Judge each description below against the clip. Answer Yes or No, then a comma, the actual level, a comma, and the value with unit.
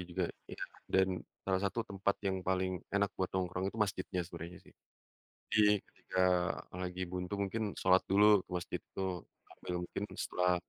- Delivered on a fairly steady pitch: Yes, narrow, 1.6 semitones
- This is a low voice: Yes, very low, 95 Hz